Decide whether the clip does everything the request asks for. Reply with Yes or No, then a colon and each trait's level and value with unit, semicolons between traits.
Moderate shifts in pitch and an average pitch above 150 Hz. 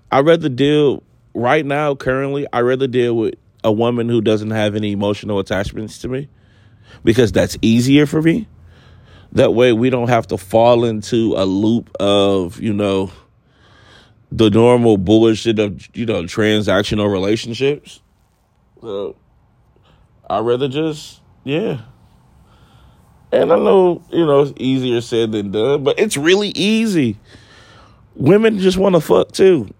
No: average, 4.3 semitones; low, 115 Hz